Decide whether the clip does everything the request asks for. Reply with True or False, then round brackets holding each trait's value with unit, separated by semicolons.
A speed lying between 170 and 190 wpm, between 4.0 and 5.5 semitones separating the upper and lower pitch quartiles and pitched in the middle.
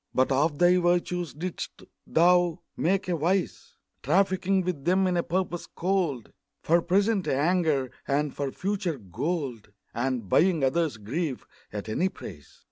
False (140 wpm; 5.1 semitones; 170 Hz)